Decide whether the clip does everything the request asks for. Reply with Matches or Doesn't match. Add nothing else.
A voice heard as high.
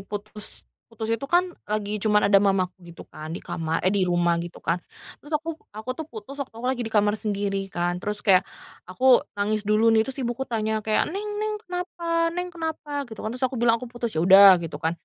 Matches